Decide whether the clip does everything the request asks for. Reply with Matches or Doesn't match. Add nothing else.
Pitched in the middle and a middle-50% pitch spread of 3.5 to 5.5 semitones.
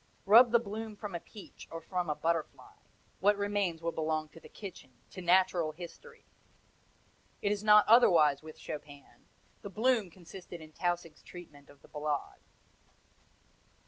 Matches